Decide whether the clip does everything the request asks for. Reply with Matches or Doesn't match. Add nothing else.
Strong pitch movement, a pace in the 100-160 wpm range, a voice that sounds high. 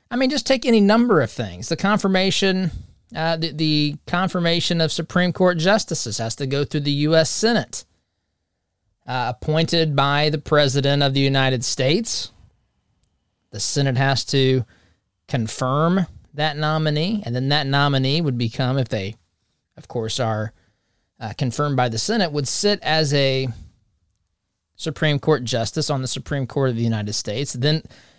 Doesn't match